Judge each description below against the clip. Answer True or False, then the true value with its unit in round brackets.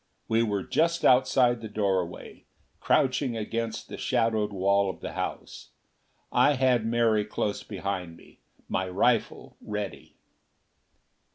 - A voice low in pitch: True (110 Hz)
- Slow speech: True (120 wpm)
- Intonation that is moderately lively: True (3.4 semitones)